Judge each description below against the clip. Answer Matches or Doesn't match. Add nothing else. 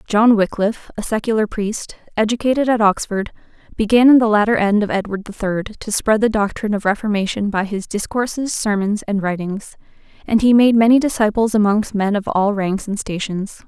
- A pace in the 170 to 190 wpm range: Matches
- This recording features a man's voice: Doesn't match